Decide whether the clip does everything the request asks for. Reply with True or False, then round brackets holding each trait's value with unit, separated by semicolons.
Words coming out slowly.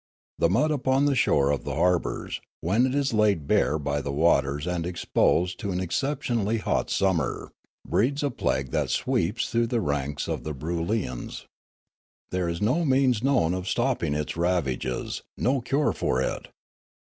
False (165 wpm)